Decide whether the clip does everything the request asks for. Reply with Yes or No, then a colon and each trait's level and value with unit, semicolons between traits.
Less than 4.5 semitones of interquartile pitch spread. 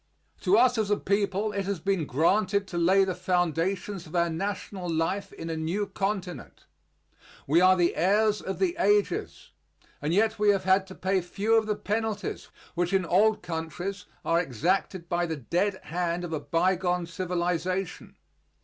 Yes: average, 2.8 semitones